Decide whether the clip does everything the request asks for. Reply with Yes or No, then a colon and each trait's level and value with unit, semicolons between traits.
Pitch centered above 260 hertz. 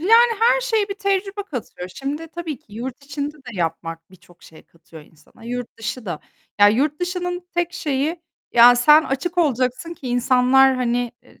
Yes: very high, 270 Hz